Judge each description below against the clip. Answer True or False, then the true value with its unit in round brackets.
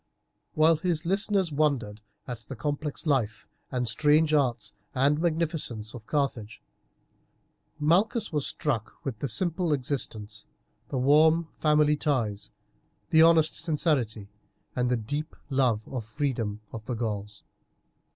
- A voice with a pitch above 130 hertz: True (140 Hz)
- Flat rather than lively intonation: False (5.3 semitones)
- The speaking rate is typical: False (125 wpm)